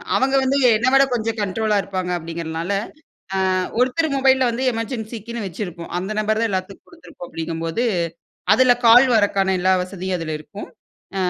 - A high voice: Yes, high, 210 Hz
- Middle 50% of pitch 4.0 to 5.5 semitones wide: Yes, average, 4.8 semitones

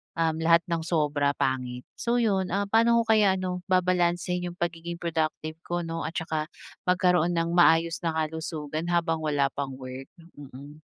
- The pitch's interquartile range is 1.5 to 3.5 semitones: Yes, narrow, 2.6 semitones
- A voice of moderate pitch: Yes, medium, 165 Hz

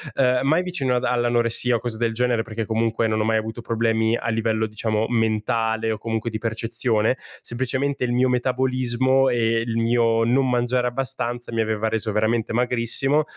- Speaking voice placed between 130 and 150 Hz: No, low, 115 Hz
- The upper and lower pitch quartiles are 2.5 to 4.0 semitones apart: No, narrow, 1.9 semitones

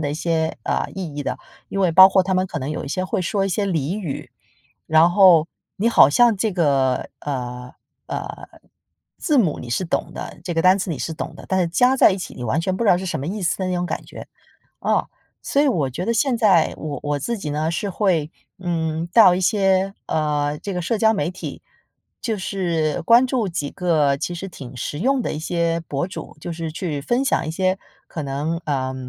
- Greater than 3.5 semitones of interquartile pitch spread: Yes, average, 4.2 semitones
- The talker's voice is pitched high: No, medium, 175 Hz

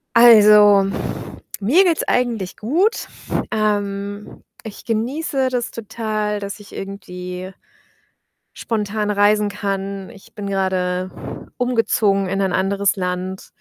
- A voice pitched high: Yes, high, 205 Hz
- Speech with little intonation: Yes, narrow, 2.3 semitones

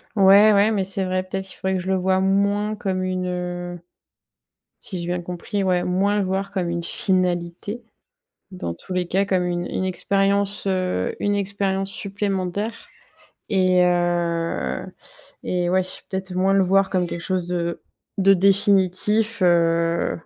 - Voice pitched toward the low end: No, medium, 185 Hz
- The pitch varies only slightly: Yes, narrow, 1.8 semitones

